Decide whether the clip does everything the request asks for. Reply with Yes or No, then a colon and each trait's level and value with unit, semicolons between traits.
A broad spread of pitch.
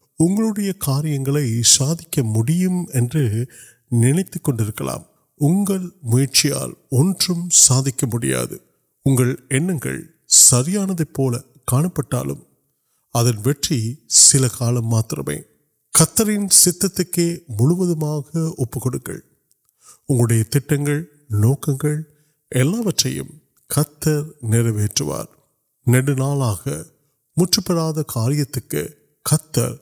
No: average, 4.8 semitones